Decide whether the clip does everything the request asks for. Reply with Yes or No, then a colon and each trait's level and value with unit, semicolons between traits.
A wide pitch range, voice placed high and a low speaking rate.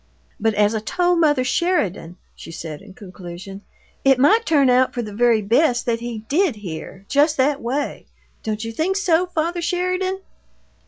No: wide, 7.8 semitones; very high, 250 Hz; average, 170 wpm